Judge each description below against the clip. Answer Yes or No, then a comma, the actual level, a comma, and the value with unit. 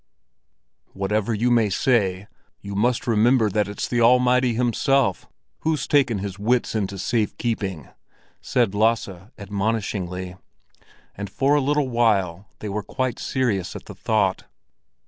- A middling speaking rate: No, slow, 130 wpm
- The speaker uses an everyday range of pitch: Yes, average, 3.8 semitones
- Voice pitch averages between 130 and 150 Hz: No, low, 110 Hz